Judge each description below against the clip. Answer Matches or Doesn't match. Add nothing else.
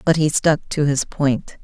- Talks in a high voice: Doesn't match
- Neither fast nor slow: Doesn't match